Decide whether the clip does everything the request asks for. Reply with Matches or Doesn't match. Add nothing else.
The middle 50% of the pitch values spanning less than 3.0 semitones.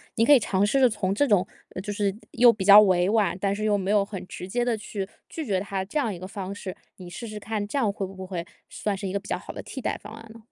Matches